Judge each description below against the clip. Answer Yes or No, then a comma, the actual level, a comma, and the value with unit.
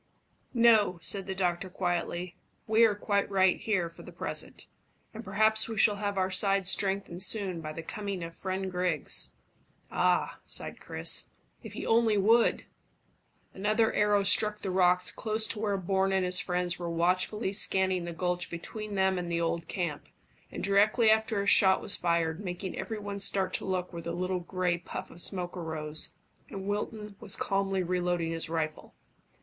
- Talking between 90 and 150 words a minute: No, average, 175 wpm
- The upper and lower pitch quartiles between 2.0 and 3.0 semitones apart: Yes, narrow, 2.5 semitones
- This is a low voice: No, high, 190 Hz